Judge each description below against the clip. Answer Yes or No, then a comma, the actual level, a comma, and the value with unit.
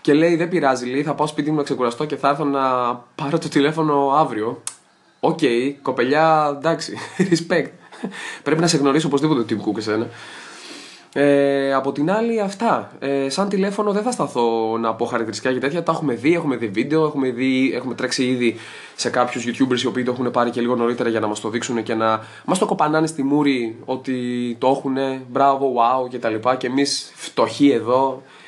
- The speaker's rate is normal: No, fast, 195 wpm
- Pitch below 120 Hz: No, low, 135 Hz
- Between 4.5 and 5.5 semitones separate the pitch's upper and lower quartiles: No, average, 3.7 semitones